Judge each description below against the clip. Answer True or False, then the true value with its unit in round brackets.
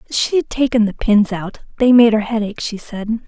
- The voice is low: False (225 Hz)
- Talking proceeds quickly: True (220 wpm)